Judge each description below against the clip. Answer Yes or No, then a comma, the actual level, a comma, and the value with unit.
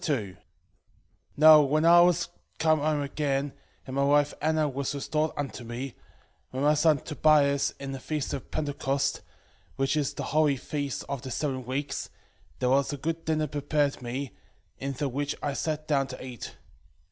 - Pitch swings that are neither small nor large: No, narrow, 2.1 semitones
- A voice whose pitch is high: No, medium, 145 Hz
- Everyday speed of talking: Yes, average, 170 wpm